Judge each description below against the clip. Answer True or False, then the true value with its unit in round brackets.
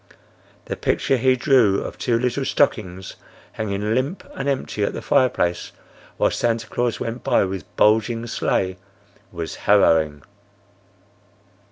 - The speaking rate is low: True (130 wpm)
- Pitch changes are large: False (4.7 semitones)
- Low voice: True (115 Hz)